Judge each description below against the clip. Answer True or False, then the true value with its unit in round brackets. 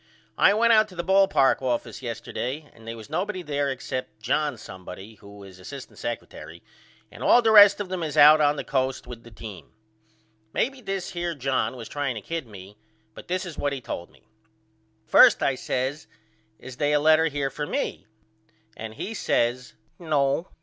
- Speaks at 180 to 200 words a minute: True (190 wpm)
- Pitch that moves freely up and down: True (6.2 semitones)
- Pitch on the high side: False (140 Hz)